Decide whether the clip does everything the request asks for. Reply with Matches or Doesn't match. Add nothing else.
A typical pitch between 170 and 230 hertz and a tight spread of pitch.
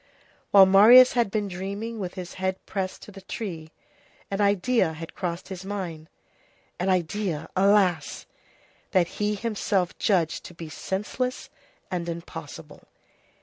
Doesn't match